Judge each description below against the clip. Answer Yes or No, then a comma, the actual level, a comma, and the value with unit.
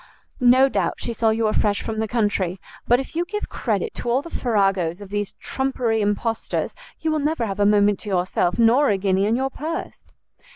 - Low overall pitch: No, high, 225 Hz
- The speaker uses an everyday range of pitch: Yes, average, 4.5 semitones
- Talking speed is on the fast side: Yes, fast, 210 wpm